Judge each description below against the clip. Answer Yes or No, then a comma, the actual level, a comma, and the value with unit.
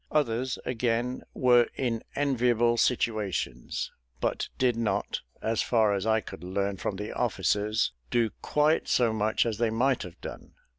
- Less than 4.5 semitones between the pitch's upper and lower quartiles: Yes, average, 2.7 semitones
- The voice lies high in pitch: No, low, 115 Hz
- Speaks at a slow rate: No, average, 150 wpm